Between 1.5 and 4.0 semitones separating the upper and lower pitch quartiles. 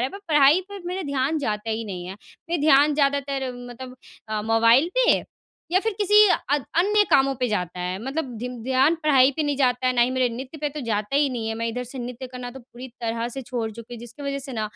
Yes: average, 3.6 semitones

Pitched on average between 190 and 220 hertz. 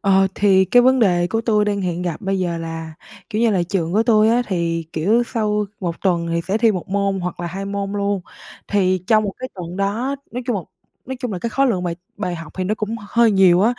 Yes: high, 195 Hz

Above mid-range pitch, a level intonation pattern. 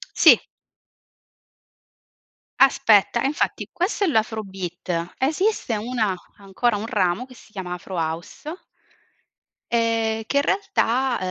No: high, 225 Hz; wide, 5.5 semitones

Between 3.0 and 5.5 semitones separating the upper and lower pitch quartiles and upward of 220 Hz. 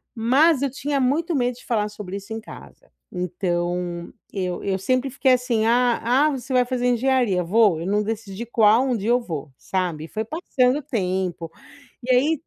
Yes: average, 5.2 semitones; high, 230 Hz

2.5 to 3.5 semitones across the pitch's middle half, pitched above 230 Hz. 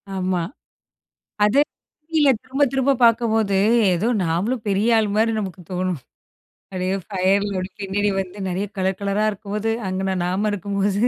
No: average, 2.9 semitones; high, 200 Hz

